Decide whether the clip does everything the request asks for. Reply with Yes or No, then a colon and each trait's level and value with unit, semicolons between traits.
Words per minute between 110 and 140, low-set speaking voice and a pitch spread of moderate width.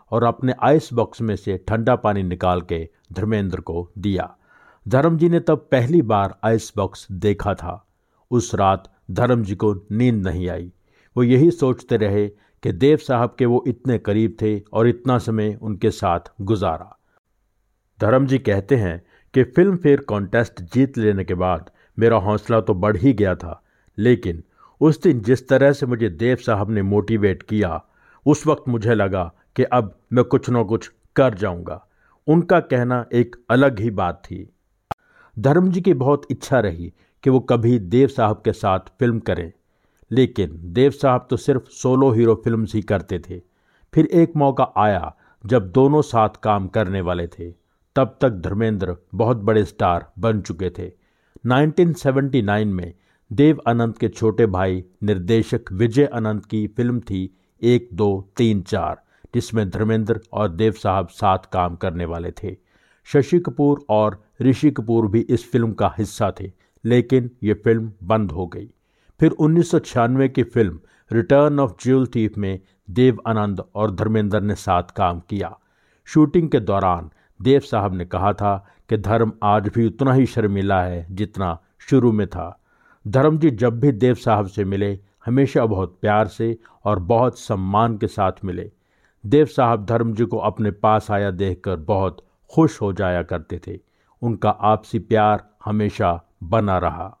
No: average, 165 wpm; low, 110 Hz; average, 4.4 semitones